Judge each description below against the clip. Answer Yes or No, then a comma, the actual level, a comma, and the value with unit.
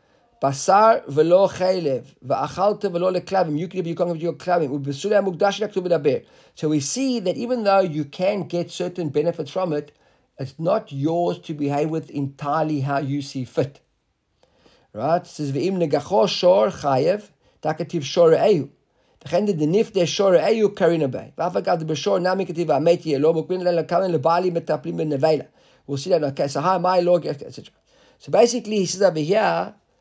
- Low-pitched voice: No, medium, 170 Hz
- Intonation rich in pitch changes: No, average, 3.5 semitones